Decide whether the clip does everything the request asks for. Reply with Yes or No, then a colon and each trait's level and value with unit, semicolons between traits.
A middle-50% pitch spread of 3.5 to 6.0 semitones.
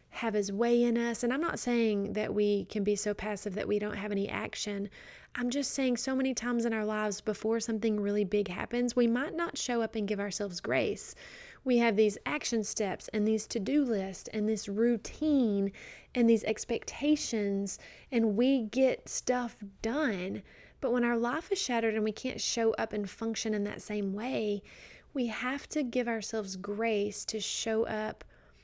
No: average, 2.8 semitones